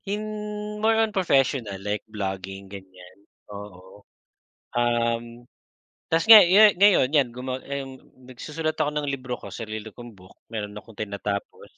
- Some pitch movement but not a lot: No, wide, 7.6 semitones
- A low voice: Yes, low, 120 Hz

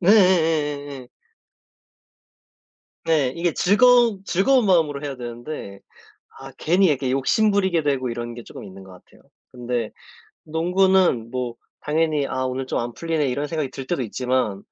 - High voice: No, medium, 145 Hz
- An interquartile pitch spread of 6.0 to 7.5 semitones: No, wide, 5.6 semitones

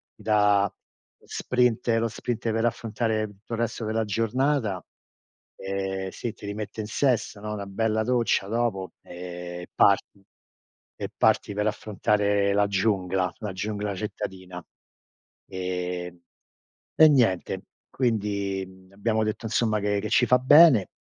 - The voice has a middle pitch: No, low, 105 Hz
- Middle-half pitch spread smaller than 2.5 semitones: No, average, 2.8 semitones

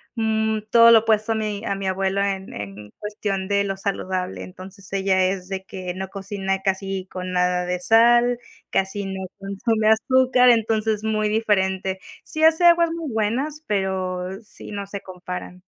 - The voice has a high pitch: Yes, high, 200 Hz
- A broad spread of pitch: No, narrow, 2.6 semitones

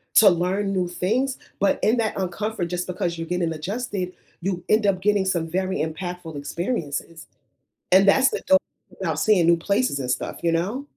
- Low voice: No, medium, 185 Hz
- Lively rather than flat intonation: No, average, 3.3 semitones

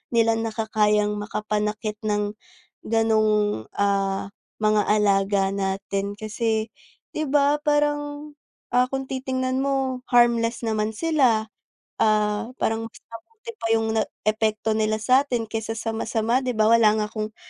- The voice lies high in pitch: Yes, high, 220 Hz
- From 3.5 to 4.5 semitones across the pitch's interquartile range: No, average, 3.0 semitones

